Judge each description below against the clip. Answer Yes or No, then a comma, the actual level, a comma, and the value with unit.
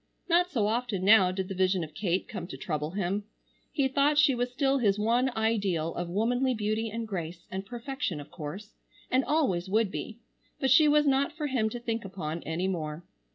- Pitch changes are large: Yes, wide, 5.8 semitones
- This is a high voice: Yes, high, 215 Hz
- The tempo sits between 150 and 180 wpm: No, average, 200 wpm